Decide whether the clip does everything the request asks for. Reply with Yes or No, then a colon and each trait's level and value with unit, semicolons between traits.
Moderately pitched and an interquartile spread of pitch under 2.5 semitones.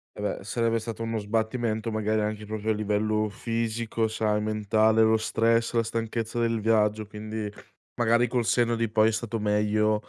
No: low, 110 Hz; narrow, 1.2 semitones